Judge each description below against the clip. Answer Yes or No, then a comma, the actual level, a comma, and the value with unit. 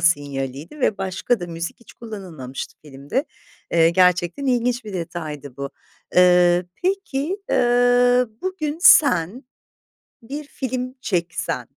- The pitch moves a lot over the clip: Yes, wide, 7.2 semitones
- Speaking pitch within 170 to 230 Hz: Yes, high, 190 Hz